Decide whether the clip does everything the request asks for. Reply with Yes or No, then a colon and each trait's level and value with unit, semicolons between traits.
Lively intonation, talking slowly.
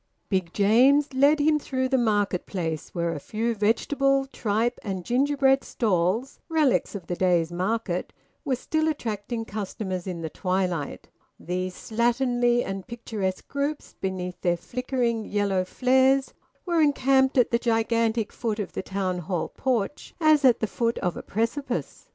No: wide, 5.8 semitones; average, 150 wpm